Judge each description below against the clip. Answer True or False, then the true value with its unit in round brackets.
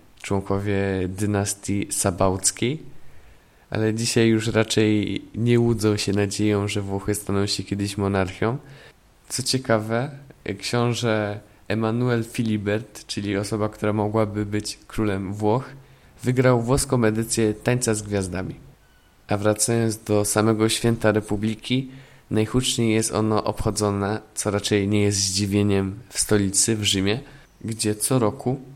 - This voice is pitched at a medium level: False (105 Hz)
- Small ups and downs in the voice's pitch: True (2.2 semitones)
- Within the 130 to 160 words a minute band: False (120 wpm)